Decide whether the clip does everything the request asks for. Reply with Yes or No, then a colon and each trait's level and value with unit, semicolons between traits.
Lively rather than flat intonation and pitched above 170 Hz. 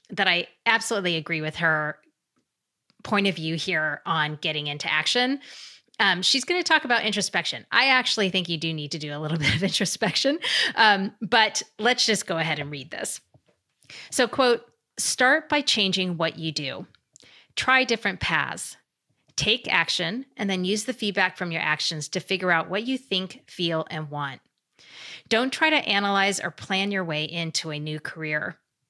Yes: wide, 5.9 semitones; high, 190 Hz